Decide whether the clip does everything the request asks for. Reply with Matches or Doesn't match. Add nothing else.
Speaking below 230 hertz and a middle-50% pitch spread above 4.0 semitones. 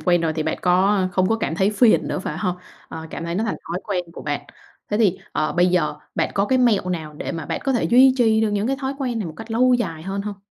Matches